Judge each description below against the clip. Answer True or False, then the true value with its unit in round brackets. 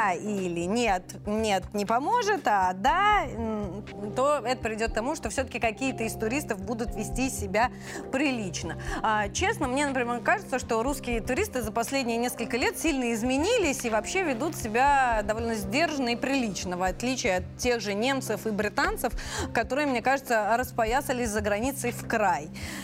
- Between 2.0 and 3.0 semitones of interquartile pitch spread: False (3.7 semitones)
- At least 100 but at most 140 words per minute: False (155 wpm)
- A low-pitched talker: False (240 Hz)